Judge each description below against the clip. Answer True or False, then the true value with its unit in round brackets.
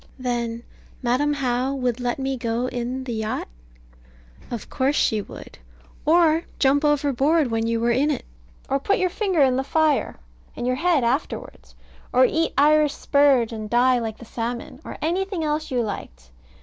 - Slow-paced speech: False (170 wpm)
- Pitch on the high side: True (260 Hz)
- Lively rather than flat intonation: False (3.8 semitones)